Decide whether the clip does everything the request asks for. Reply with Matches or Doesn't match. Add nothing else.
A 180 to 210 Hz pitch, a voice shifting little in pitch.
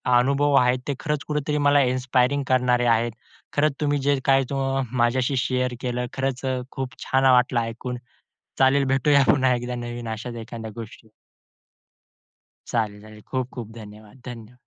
Doesn't match